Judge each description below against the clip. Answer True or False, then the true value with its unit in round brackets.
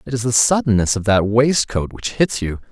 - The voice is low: True (115 Hz)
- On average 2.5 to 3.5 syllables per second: False (5.2 syllables/s)